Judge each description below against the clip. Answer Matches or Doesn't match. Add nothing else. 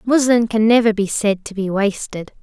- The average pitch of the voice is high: Matches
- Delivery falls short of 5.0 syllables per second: Matches